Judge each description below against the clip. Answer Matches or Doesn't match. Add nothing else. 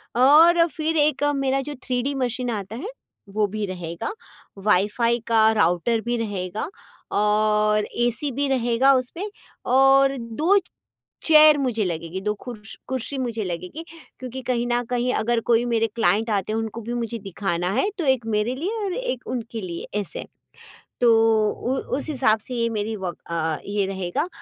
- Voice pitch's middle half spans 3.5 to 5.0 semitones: Matches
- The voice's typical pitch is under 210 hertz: Doesn't match